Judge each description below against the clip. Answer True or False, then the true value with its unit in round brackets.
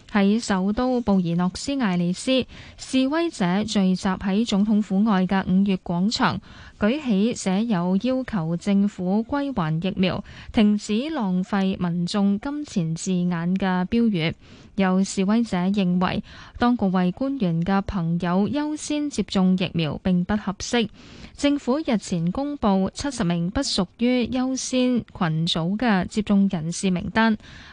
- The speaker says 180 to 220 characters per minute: True (210 characters per minute)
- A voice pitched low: False (200 Hz)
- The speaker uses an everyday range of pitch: True (4.2 semitones)